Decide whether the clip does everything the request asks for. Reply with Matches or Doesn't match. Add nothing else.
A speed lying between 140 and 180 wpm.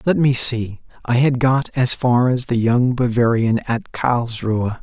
Matches